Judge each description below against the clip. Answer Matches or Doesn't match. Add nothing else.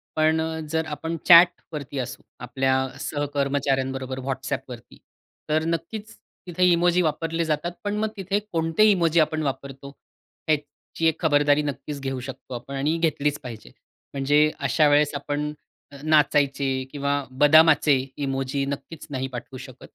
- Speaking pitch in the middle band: Matches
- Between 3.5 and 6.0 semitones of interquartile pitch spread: Doesn't match